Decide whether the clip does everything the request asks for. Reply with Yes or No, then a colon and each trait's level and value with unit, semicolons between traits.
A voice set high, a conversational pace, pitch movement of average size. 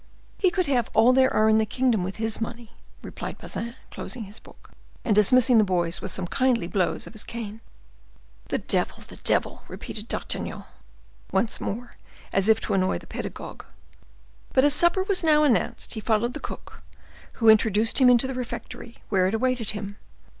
Yes: high, 225 Hz; average, 180 wpm; average, 3.3 semitones